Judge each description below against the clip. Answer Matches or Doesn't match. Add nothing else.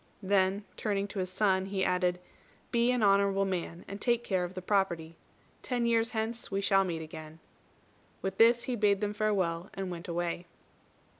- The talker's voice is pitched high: Matches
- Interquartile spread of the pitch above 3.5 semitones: Doesn't match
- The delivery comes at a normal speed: Matches